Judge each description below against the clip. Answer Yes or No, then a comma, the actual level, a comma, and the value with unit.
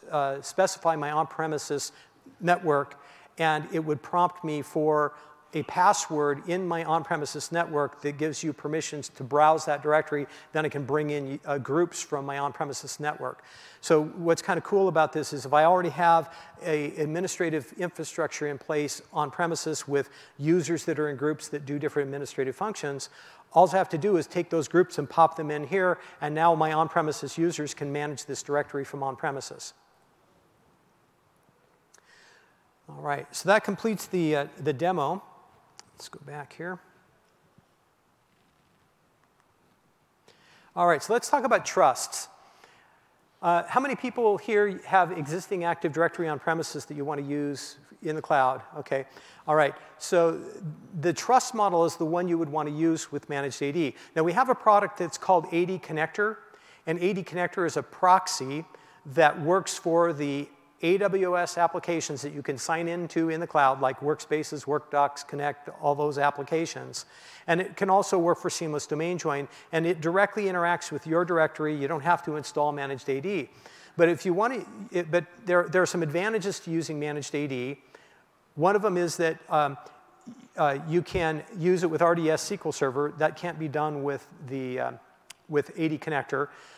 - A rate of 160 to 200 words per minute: Yes, average, 175 wpm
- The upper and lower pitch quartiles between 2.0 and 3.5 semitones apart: Yes, average, 3.1 semitones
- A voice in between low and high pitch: Yes, medium, 160 Hz